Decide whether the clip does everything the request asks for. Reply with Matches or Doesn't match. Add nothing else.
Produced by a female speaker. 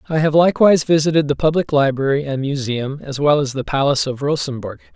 Doesn't match